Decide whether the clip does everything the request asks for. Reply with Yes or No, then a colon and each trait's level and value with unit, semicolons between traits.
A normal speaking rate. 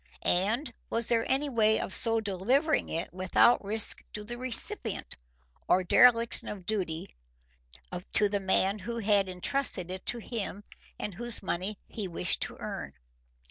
Yes: average, 150 wpm